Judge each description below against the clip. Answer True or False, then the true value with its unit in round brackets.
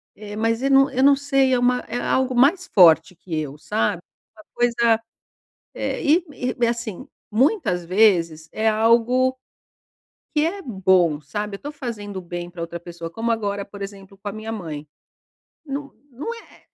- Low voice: False (220 Hz)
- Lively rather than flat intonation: True (6.1 semitones)